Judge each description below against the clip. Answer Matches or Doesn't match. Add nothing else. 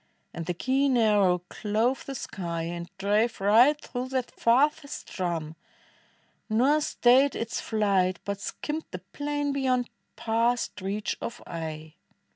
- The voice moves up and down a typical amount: Doesn't match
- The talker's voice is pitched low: Doesn't match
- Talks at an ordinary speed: Doesn't match